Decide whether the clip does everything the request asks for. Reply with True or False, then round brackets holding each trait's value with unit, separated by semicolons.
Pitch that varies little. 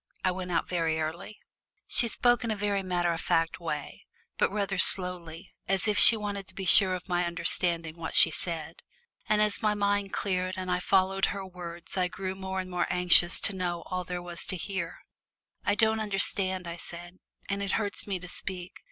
True (2.3 semitones)